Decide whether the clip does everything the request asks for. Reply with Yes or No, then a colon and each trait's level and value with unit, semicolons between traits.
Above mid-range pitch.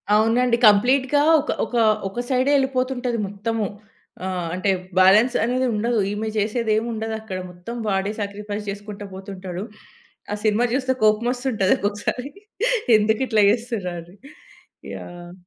Yes: high, 215 Hz